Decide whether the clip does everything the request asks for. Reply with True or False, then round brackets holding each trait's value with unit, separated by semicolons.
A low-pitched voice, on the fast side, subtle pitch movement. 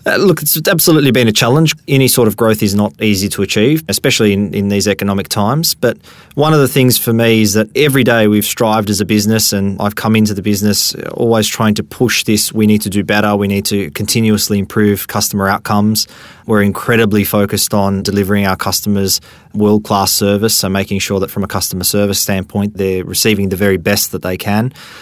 True (105 Hz; 210 wpm; 2.0 semitones)